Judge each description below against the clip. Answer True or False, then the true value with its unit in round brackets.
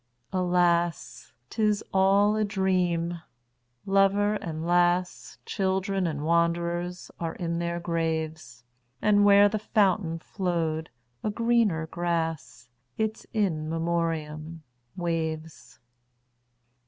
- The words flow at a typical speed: False (85 wpm)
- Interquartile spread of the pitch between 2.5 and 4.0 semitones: True (3.2 semitones)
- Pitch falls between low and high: True (170 Hz)